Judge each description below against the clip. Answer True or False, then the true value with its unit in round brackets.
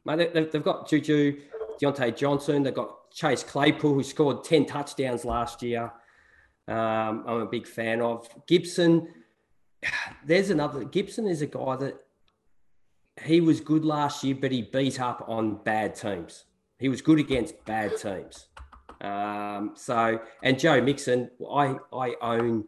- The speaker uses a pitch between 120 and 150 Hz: True (135 Hz)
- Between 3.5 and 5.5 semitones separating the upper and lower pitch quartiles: True (4.6 semitones)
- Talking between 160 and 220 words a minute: False (150 wpm)